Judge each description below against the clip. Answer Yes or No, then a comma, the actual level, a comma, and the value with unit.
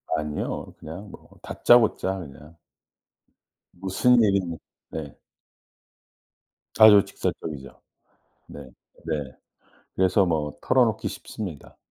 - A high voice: No, very low, 90 Hz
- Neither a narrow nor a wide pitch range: Yes, average, 5.0 semitones